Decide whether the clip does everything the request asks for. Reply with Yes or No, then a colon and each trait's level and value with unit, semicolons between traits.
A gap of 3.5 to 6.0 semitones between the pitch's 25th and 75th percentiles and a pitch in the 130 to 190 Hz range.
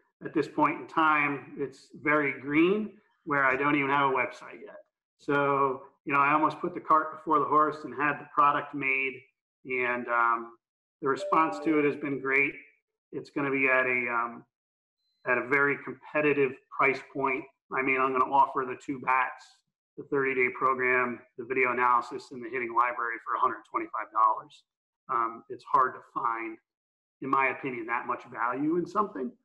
No: average, 2.9 semitones; medium, 140 Hz